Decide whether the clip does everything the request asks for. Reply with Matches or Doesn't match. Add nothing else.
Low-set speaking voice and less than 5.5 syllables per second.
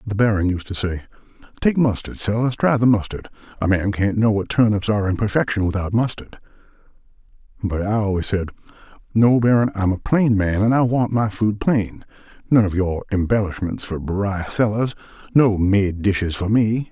Matches